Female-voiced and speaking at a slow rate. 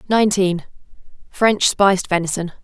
Yes: female; slow, 70 wpm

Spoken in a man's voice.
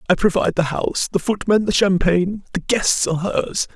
Yes: male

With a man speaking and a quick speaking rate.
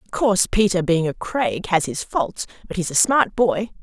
No: female; fast, 220 wpm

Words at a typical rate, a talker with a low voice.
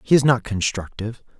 Yes: average, 170 wpm; low, 115 Hz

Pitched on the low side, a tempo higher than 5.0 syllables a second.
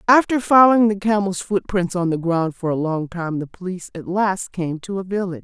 No: high, 190 Hz; 5.5 syllables/s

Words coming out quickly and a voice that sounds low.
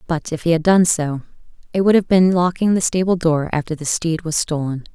No: fast, 230 wpm; medium, 165 Hz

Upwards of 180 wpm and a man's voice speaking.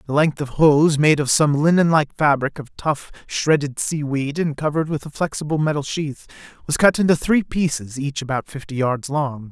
Yes: average, 190 wpm; male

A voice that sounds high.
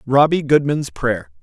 No: low, 135 Hz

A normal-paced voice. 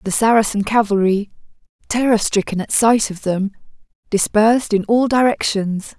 No: slow, 130 wpm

